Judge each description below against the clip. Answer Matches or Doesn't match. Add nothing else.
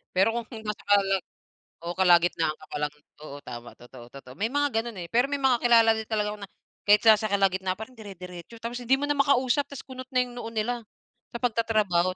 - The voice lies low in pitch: Doesn't match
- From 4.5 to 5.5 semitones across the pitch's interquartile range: Matches